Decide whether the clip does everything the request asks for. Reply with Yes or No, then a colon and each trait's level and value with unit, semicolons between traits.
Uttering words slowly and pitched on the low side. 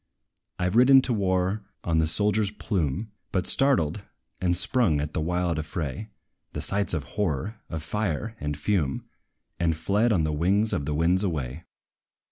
No: average, 165 wpm; very low, 90 Hz